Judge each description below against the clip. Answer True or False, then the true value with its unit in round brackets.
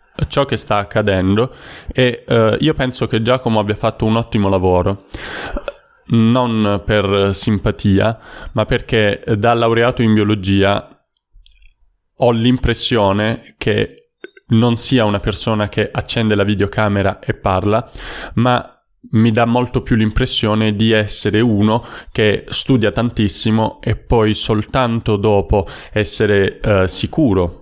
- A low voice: True (110 Hz)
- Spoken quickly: False (120 wpm)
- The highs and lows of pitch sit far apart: False (2.6 semitones)